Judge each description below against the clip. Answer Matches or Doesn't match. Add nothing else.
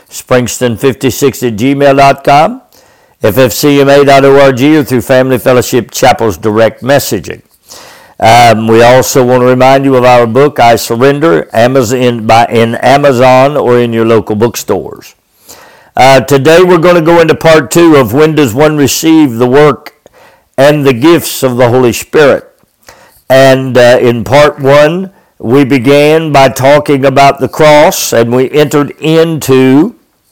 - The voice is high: Doesn't match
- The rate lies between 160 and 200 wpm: Doesn't match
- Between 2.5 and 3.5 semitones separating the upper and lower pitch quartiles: Matches